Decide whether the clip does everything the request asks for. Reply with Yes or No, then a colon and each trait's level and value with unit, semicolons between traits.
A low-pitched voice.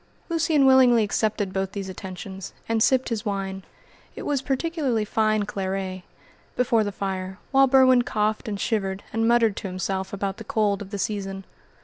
No: high, 210 Hz